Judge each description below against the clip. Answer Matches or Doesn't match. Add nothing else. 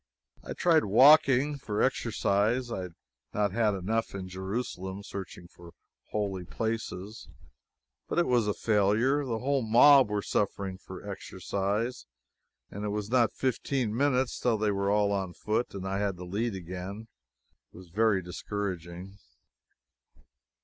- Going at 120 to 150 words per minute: Matches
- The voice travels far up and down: Doesn't match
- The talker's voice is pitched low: Matches